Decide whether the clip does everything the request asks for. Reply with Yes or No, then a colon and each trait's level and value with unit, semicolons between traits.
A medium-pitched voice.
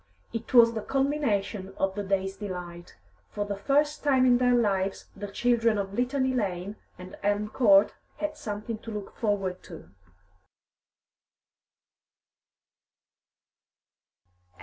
No: high, 210 Hz